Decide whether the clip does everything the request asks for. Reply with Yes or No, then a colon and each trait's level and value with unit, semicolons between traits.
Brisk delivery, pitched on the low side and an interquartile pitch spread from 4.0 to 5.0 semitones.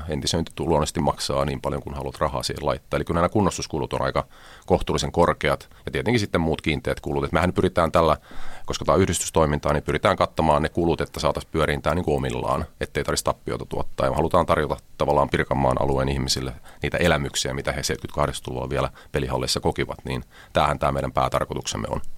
No: fast, 185 wpm; very low, 75 Hz; average, 3.3 semitones